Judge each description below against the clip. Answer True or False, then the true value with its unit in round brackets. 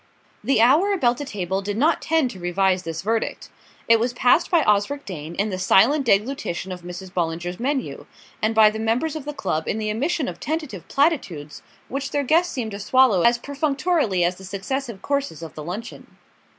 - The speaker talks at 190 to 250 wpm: True (195 wpm)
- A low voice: False (225 Hz)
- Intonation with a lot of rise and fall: True (6.9 semitones)